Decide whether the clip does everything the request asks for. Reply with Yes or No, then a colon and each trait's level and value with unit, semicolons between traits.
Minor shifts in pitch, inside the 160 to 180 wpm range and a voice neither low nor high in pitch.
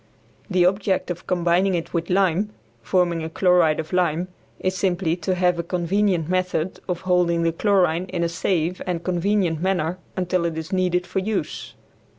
Yes: narrow, 1.7 semitones; average, 170 wpm; medium, 180 Hz